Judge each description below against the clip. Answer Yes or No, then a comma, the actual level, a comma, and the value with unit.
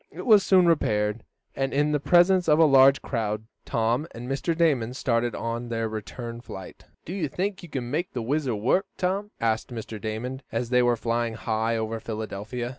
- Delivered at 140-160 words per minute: No, average, 190 wpm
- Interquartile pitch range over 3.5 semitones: Yes, average, 4.9 semitones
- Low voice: Yes, low, 120 Hz